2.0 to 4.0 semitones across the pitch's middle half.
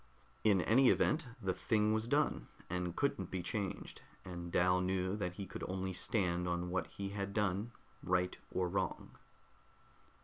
Yes: average, 2.7 semitones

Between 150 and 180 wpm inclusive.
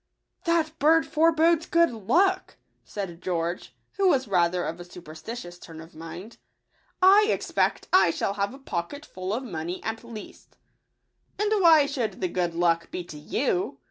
Yes: average, 175 wpm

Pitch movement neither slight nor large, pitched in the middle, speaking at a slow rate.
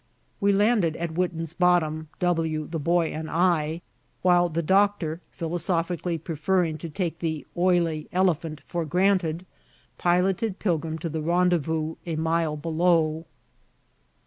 No: narrow, 2.1 semitones; medium, 170 Hz; slow, 125 wpm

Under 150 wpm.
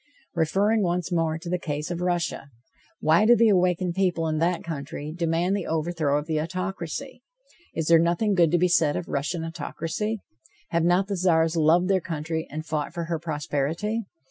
No: average, 185 wpm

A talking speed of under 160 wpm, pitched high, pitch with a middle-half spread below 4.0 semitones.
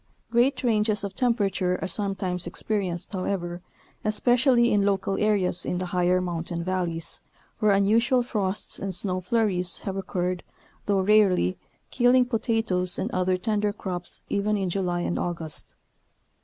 Yes: average, 140 wpm; high, 195 Hz; average, 2.9 semitones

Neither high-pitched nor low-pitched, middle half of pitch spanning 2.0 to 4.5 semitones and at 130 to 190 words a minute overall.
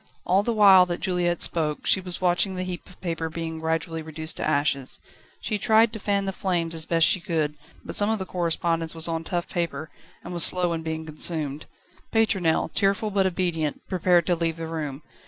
No: medium, 170 Hz; narrow, 2.6 semitones; fast, 205 wpm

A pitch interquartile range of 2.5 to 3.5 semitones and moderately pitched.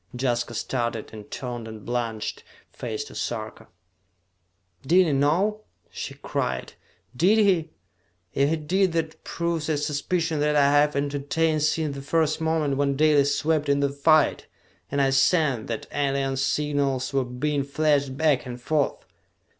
Yes: average, 2.9 semitones; medium, 145 Hz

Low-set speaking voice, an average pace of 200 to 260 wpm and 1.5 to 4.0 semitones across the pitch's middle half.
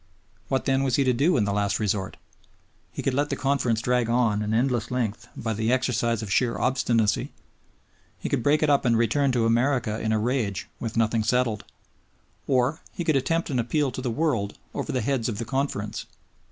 Yes: low, 120 Hz; fast, 205 wpm; average, 3.3 semitones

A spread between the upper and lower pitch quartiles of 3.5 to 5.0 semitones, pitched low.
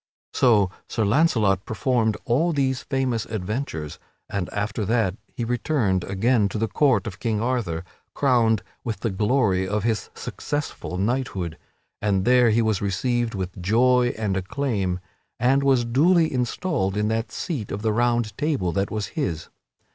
Yes: average, 4.3 semitones; low, 110 Hz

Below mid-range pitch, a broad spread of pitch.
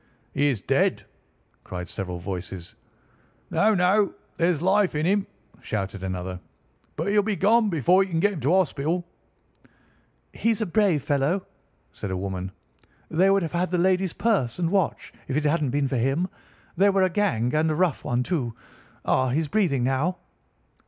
No: medium, 160 Hz; wide, 7.1 semitones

